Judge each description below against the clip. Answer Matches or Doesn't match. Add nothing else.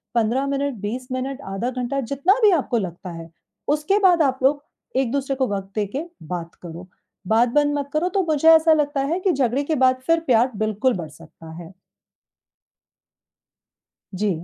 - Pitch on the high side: Matches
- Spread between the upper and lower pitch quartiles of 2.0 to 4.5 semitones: Doesn't match